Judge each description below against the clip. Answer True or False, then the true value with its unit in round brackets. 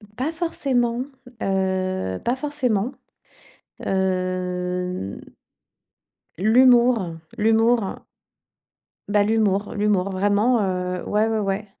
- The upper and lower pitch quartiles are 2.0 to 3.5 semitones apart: False (4.1 semitones)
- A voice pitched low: False (205 Hz)